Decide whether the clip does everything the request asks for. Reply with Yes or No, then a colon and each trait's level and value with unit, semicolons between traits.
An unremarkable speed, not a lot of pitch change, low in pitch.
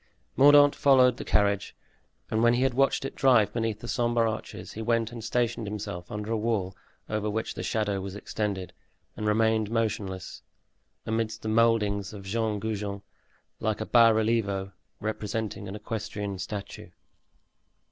Yes: average, 155 wpm; narrow, 2.1 semitones; low, 110 Hz